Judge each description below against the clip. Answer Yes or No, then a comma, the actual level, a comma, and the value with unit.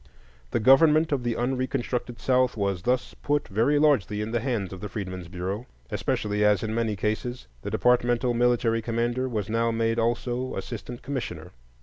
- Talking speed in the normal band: Yes, average, 165 wpm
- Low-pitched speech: Yes, low, 120 Hz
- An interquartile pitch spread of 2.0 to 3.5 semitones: Yes, average, 3.1 semitones